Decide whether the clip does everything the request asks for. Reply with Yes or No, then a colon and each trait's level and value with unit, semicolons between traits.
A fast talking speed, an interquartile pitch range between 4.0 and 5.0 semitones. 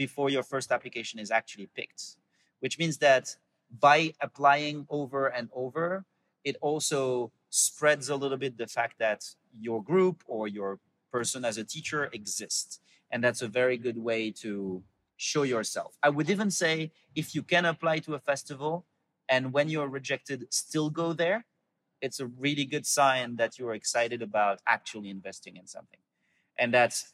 Yes: fast, 165 wpm; average, 4.6 semitones